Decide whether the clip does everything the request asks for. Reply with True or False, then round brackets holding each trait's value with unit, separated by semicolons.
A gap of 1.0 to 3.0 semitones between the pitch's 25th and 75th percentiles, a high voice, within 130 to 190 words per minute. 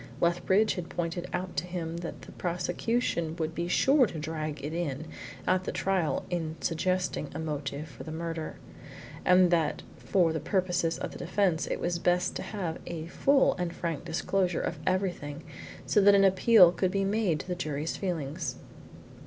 False (2.5 semitones; 175 Hz; 175 wpm)